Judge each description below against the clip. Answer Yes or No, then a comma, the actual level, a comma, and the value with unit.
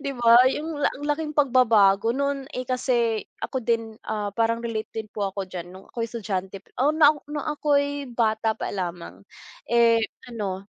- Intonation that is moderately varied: Yes, average, 5.0 semitones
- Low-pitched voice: No, high, 230 Hz